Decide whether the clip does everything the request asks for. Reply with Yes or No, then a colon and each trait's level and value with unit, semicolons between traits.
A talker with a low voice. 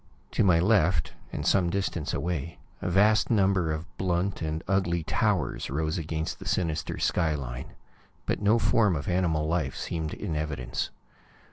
Yes: very low, 85 Hz